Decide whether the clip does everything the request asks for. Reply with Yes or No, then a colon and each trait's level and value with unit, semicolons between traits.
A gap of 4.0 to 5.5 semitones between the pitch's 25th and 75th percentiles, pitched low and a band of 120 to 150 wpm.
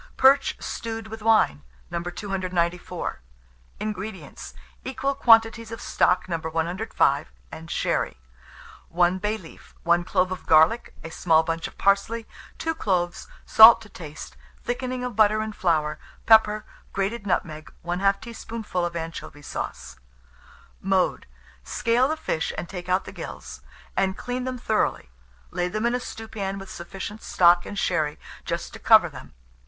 No: average, 4.6 semitones; high, 195 Hz; average, 145 wpm